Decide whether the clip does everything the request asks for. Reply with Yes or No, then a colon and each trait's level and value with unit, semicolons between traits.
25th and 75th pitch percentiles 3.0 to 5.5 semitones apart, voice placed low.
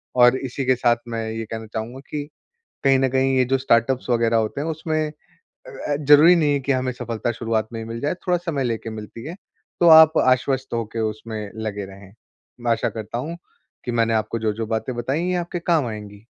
Yes: average, 4.1 semitones; low, 120 Hz